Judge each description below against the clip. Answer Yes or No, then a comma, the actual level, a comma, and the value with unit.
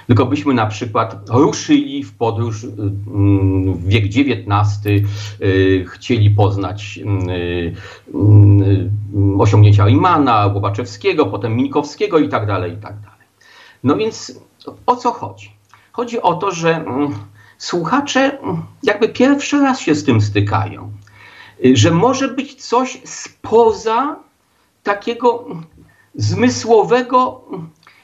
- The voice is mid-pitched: No, low, 115 Hz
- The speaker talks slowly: Yes, slow, 100 wpm